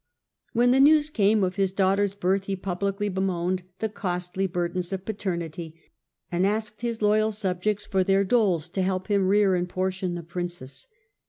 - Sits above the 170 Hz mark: Yes, high, 190 Hz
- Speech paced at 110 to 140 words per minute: No, average, 170 wpm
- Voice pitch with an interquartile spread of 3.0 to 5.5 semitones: No, narrow, 2.4 semitones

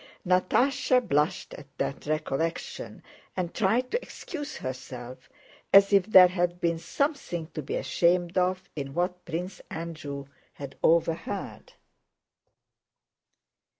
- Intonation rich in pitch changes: No, average, 3.7 semitones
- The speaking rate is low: Yes, slow, 115 wpm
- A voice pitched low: No, medium, 175 Hz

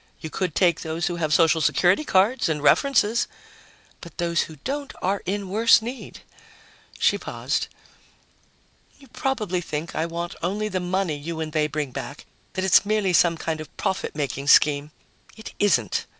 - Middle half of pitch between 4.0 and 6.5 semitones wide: Yes, average, 4.6 semitones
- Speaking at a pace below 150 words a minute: No, average, 175 wpm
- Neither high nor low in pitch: Yes, medium, 175 Hz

